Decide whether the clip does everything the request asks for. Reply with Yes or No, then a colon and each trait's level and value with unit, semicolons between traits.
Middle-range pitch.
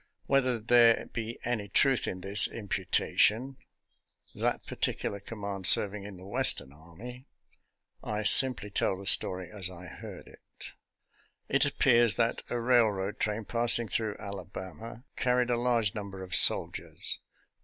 No: low, 105 Hz